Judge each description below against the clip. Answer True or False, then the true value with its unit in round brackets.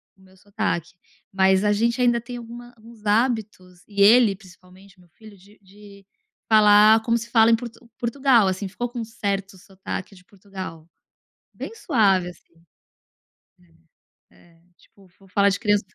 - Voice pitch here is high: True (205 Hz)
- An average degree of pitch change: True (3.1 semitones)